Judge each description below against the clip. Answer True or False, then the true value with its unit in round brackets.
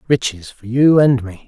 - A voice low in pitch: True (120 Hz)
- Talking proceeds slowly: False (205 wpm)